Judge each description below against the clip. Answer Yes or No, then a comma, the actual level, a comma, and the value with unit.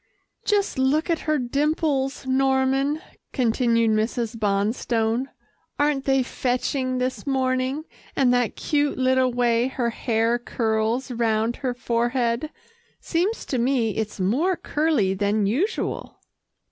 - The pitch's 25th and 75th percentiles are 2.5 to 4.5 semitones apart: Yes, average, 2.9 semitones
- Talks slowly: Yes, slow, 120 wpm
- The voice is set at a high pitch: Yes, very high, 255 Hz